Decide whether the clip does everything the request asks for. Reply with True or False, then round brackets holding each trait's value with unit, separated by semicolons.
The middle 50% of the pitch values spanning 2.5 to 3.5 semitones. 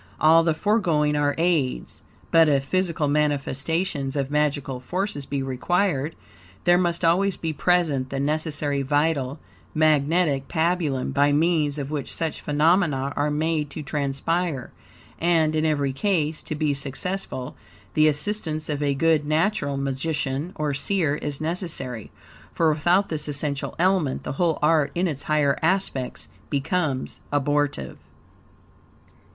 True (2.8 semitones)